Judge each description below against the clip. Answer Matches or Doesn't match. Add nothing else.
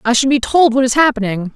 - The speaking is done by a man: Doesn't match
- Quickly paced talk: Matches